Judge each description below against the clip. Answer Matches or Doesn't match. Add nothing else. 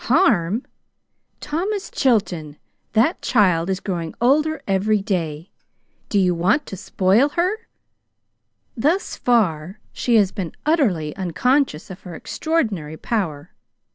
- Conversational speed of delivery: Doesn't match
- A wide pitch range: Matches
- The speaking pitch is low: Doesn't match